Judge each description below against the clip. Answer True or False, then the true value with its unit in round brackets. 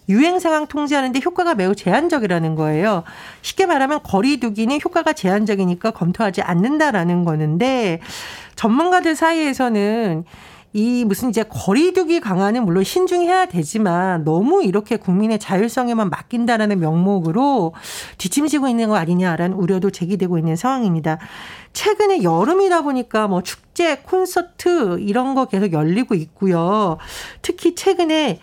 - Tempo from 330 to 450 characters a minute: True (345 characters per minute)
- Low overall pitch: False (220 Hz)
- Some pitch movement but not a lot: False (8.3 semitones)